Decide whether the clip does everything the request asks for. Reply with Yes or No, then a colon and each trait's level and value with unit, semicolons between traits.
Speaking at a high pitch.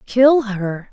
Yes: high, 225 Hz